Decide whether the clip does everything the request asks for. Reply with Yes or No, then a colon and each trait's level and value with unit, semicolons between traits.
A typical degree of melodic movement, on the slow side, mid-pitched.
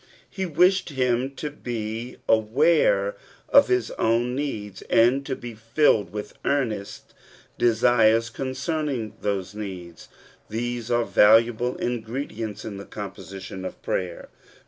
No: average, 3.5 semitones; slow, 125 wpm; low, 115 Hz